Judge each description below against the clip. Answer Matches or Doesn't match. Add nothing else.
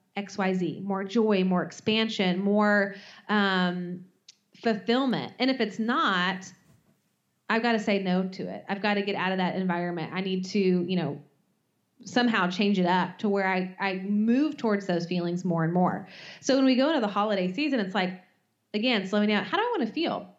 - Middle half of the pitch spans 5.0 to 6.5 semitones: Doesn't match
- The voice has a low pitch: Doesn't match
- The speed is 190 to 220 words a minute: Matches